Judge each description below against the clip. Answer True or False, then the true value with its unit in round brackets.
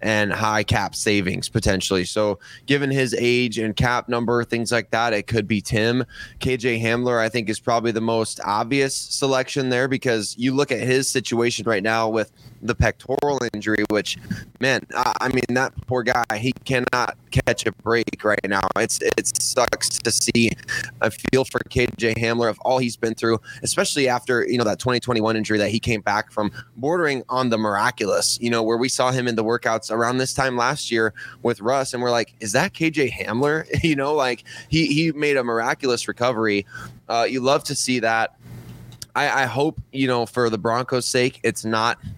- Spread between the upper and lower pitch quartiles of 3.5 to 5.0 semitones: False (2.5 semitones)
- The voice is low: True (120 Hz)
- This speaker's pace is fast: False (195 wpm)